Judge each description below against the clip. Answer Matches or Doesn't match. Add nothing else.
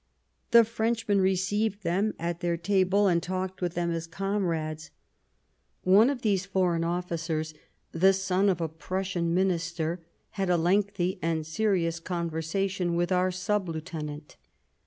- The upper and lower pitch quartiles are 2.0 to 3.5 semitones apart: Matches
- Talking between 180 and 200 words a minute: Doesn't match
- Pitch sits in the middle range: Matches